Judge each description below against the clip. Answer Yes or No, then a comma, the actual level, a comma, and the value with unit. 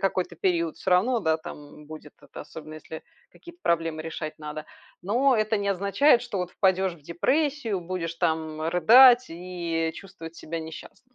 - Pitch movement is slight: No, average, 4.0 semitones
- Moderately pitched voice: Yes, medium, 175 Hz